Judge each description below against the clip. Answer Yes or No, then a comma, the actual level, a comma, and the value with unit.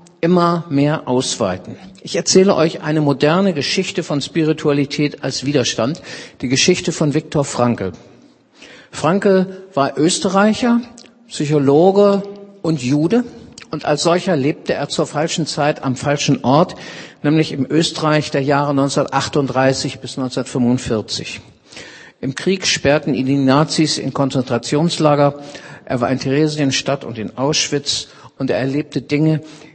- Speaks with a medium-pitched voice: Yes, medium, 150 Hz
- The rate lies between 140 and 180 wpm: No, slow, 125 wpm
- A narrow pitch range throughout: No, average, 3.6 semitones